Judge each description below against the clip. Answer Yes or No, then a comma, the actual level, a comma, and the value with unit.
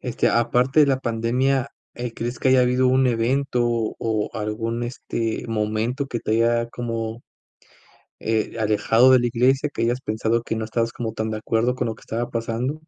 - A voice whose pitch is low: Yes, low, 115 Hz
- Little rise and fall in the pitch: Yes, narrow, 2.0 semitones